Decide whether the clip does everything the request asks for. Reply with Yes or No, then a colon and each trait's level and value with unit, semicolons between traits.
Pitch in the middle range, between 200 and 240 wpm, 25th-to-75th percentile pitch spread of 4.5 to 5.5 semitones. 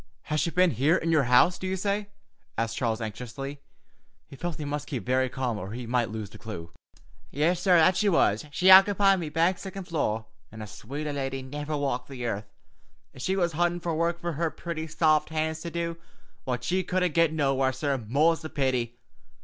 Yes: medium, 150 Hz; fast, 205 wpm; average, 5.2 semitones